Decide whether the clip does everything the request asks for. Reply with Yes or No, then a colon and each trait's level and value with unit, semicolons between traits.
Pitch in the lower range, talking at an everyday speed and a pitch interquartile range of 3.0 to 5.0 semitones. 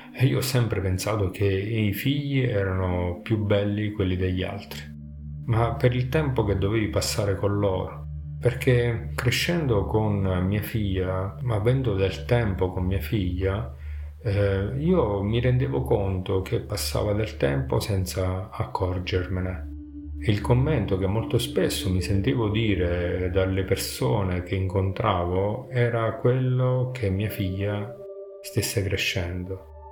Yes: low, 100 Hz; average, 130 wpm; average, 3.9 semitones